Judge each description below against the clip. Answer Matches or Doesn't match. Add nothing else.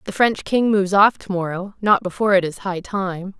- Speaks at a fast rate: Matches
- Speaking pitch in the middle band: Doesn't match